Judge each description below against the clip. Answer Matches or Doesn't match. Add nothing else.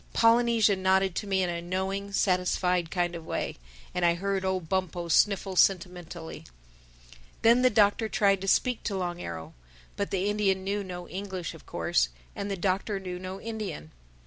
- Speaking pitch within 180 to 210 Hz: Matches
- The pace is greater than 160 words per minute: Matches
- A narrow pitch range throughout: Matches